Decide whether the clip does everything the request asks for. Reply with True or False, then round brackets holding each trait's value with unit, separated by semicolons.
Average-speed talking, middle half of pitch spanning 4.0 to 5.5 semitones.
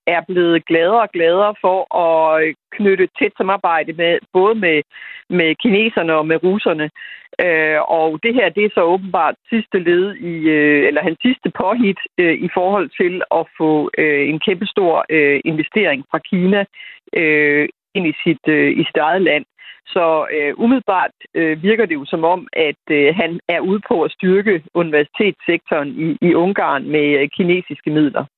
True (165 wpm; 4.4 semitones)